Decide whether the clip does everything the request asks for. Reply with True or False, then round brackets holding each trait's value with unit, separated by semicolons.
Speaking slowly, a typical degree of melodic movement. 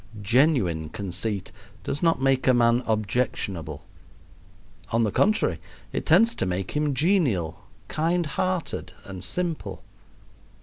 False (120 wpm; 8.5 semitones)